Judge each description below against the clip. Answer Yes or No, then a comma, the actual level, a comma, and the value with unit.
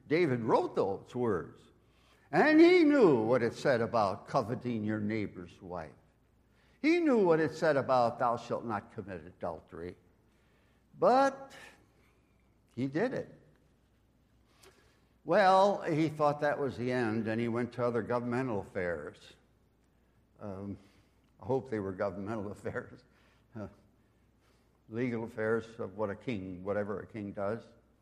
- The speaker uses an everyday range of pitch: Yes, average, 4.3 semitones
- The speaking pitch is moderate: No, low, 115 Hz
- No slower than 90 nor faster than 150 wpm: Yes, slow, 135 wpm